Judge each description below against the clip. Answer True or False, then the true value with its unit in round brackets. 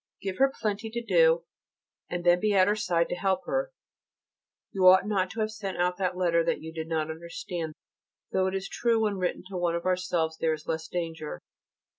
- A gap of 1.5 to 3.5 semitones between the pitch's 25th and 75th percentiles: True (3.1 semitones)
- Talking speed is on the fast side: True (210 wpm)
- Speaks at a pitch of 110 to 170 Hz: False (180 Hz)